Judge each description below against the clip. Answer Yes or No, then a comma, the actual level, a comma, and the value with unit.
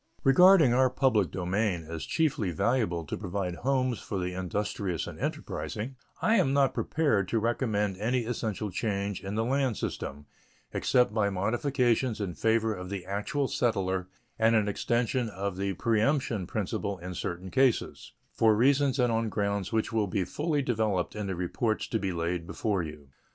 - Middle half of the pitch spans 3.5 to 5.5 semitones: Yes, average, 4.6 semitones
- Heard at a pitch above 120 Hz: No, low, 105 Hz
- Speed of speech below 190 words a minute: Yes, average, 165 wpm